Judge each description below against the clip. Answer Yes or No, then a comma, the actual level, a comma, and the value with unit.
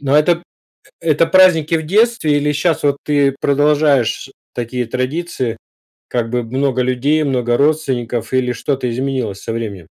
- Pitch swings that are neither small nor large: Yes, average, 3.7 semitones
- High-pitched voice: No, medium, 140 Hz